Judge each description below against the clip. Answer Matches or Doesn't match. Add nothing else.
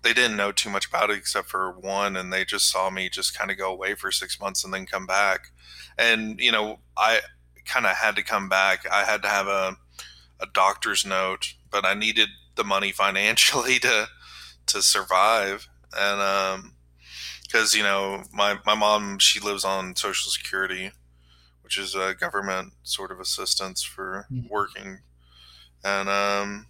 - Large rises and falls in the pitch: Matches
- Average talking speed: Matches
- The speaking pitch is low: Matches